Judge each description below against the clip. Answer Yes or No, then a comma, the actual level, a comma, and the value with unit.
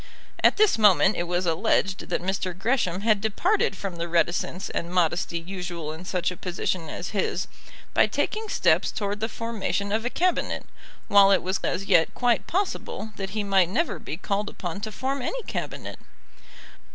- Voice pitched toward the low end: No, high, 195 Hz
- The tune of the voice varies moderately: Yes, average, 3.8 semitones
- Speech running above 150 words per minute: Yes, average, 175 wpm